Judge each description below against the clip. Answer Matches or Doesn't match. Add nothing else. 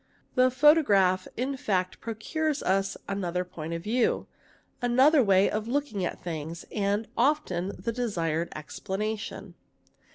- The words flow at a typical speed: Doesn't match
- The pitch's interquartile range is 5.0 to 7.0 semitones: Matches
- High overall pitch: Matches